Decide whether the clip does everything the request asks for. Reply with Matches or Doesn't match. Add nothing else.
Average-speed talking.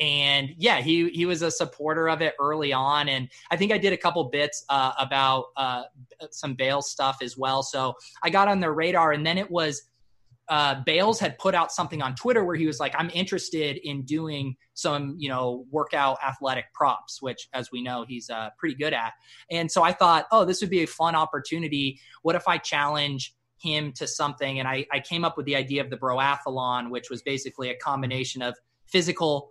Doesn't match